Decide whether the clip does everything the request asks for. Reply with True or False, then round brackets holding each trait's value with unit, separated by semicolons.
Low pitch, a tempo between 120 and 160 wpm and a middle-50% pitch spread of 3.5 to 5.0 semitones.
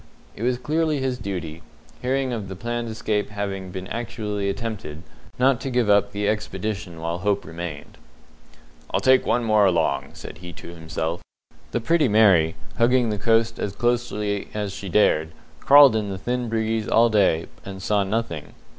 False (105 Hz; 170 wpm; 3.8 semitones)